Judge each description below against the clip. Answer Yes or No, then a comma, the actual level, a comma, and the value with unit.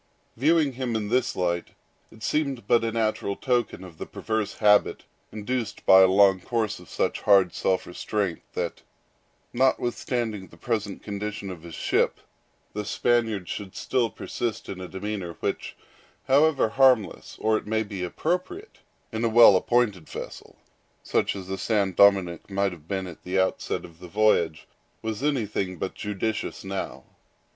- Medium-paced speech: Yes, average, 160 wpm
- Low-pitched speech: Yes, low, 105 Hz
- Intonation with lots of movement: No, average, 3.8 semitones